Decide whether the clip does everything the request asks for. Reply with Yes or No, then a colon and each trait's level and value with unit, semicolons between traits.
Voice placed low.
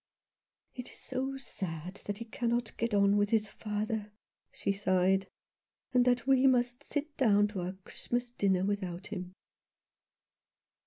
No: high, 210 Hz